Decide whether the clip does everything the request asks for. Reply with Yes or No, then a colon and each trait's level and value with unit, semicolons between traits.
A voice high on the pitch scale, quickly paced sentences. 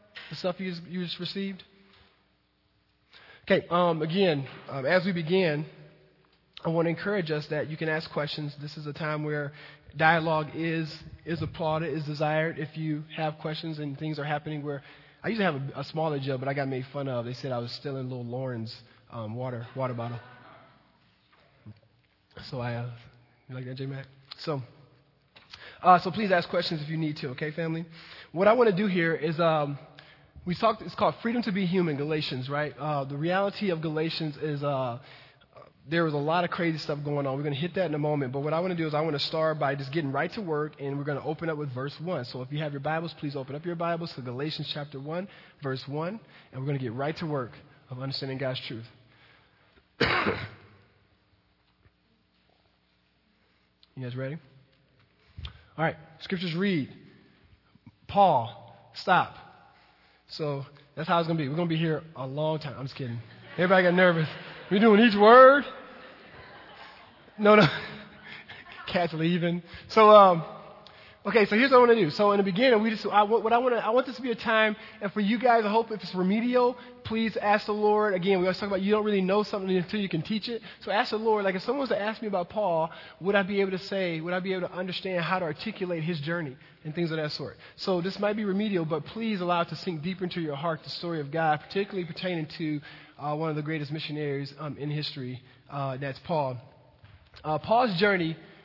No: medium, 160 Hz; fast, 210 wpm